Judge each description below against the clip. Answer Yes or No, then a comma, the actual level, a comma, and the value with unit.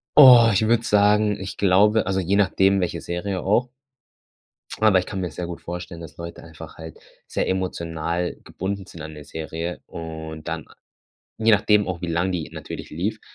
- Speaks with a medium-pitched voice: No, very low, 90 Hz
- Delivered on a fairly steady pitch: No, average, 3.6 semitones